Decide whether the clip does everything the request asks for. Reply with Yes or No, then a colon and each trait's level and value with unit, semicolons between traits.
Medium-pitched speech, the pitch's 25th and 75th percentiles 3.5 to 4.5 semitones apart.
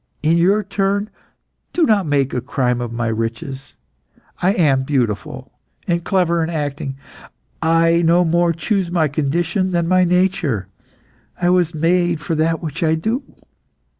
Yes: medium, 165 Hz; average, 4.1 semitones